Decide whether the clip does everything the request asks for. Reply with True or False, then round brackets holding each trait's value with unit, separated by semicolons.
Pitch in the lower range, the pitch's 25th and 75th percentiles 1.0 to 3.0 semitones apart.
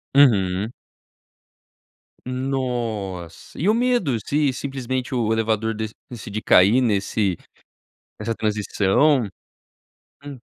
False (115 Hz; 4.1 semitones)